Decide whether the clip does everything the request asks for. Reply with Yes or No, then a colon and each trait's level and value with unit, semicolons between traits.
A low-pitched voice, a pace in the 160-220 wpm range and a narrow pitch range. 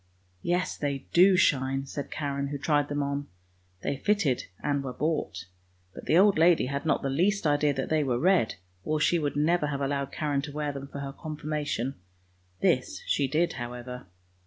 No: medium, 145 Hz; average, 190 wpm; narrow, 2.3 semitones